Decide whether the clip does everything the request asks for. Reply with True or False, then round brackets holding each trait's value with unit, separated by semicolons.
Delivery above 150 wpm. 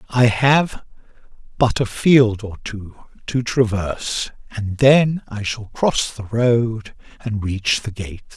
False (145 wpm)